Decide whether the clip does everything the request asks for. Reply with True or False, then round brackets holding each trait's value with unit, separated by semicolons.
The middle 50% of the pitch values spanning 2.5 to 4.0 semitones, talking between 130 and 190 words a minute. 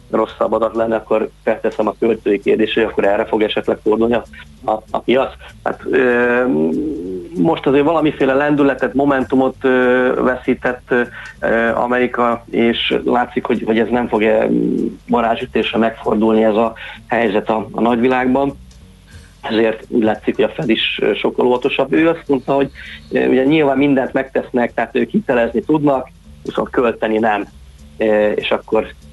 True (3.2 semitones; 140 wpm)